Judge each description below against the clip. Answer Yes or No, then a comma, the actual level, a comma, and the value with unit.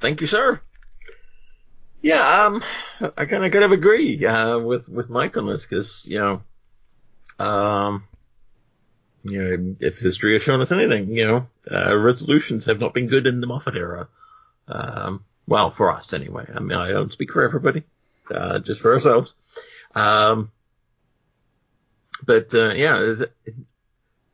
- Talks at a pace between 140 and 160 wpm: Yes, average, 155 wpm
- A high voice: No, low, 120 Hz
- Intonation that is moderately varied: No, wide, 6.6 semitones